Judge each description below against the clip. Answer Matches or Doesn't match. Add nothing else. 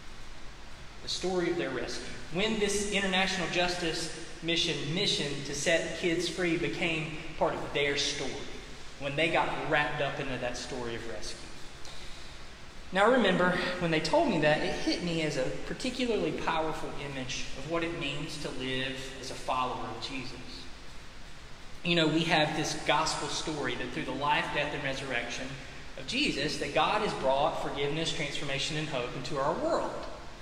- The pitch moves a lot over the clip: Doesn't match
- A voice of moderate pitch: Matches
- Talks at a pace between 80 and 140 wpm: Doesn't match